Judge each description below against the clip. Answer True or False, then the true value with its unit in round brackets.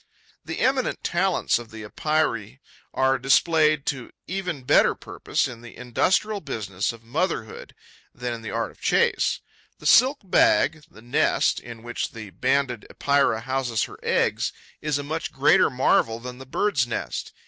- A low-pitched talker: True (130 Hz)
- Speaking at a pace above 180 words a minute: False (160 wpm)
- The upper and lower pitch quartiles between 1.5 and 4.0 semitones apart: False (5.1 semitones)